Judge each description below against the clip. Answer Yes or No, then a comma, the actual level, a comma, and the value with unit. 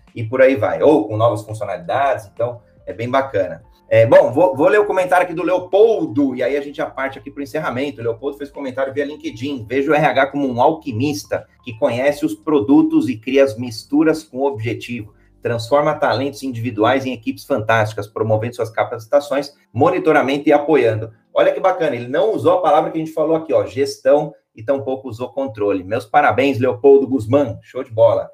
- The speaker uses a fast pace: Yes, fast, 195 wpm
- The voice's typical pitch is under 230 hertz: Yes, medium, 140 Hz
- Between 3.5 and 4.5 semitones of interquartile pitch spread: Yes, average, 4.2 semitones